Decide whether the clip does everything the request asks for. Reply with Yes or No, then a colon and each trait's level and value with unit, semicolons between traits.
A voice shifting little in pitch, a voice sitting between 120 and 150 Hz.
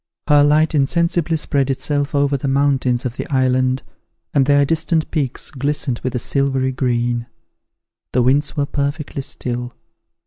Yes: narrow, 2.2 semitones; medium, 140 Hz